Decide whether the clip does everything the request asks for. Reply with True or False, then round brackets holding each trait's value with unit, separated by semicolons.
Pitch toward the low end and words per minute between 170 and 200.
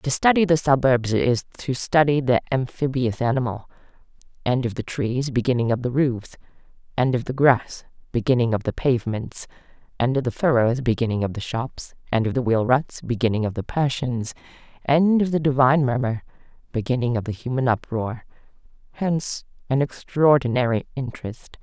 False (125 Hz; 160 wpm)